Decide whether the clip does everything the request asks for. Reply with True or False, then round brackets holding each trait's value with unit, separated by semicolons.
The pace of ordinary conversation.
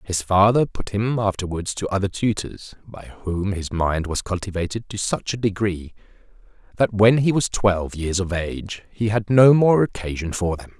True (185 wpm)